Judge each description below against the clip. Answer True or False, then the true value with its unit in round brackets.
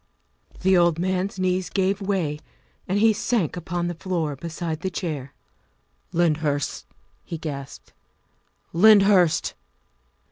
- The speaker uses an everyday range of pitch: True (3.2 semitones)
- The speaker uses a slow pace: True (120 wpm)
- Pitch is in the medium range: True (175 Hz)